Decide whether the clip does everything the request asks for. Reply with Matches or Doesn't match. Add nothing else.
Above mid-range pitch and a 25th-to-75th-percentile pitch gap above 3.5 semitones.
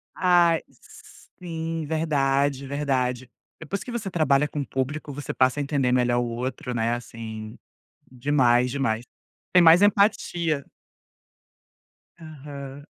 Doesn't match